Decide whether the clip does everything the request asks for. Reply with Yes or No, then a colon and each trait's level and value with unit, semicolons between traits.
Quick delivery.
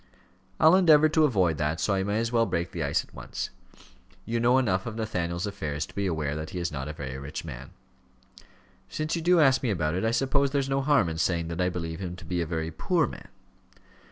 Yes: fast, 240 wpm